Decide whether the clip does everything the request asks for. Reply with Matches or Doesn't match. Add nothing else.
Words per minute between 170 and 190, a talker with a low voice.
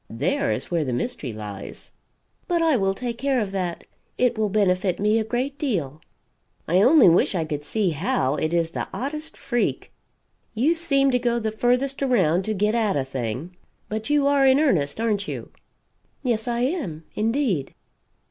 Doesn't match